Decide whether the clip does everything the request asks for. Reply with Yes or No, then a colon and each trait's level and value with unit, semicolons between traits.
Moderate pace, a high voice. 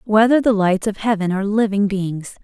Yes: average, 195 wpm; high, 205 Hz